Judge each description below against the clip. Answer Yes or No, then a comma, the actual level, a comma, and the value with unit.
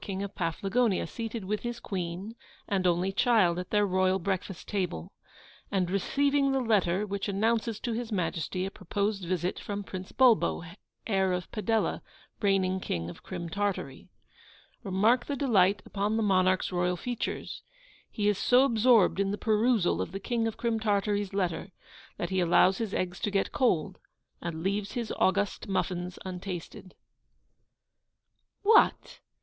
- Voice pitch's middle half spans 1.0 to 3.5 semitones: Yes, average, 3.2 semitones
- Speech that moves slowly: No, average, 155 wpm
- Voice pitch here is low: No, high, 195 Hz